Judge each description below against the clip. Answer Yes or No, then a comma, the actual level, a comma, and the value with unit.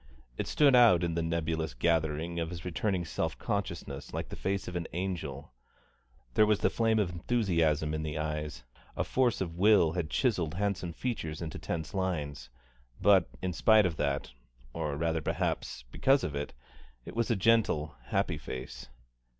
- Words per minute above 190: No, average, 170 wpm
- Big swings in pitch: No, average, 4.4 semitones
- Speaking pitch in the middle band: No, very low, 85 Hz